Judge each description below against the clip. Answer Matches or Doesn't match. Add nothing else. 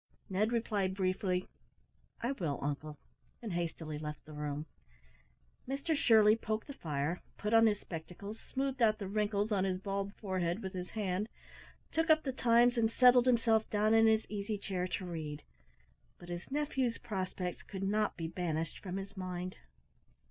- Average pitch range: Matches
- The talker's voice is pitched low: Doesn't match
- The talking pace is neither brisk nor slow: Matches